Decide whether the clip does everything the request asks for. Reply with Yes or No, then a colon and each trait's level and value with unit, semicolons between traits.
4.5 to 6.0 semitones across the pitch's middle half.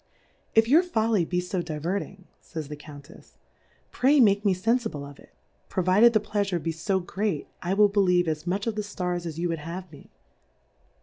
No: average, 4.1 semitones